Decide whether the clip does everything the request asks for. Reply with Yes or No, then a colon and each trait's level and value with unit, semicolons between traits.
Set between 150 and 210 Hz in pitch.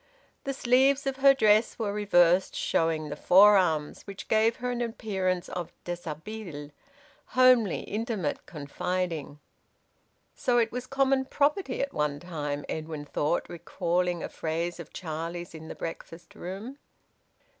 Yes: medium, 185 Hz